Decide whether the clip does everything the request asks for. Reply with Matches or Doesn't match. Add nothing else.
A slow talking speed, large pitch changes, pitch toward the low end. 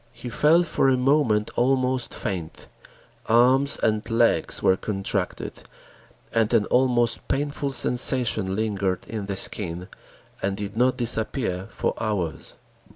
Doesn't match